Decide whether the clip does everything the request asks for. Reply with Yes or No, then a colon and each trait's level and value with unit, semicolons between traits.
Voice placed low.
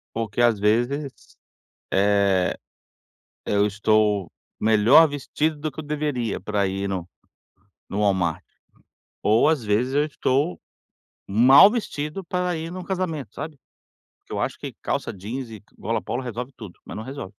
Yes: low, 120 Hz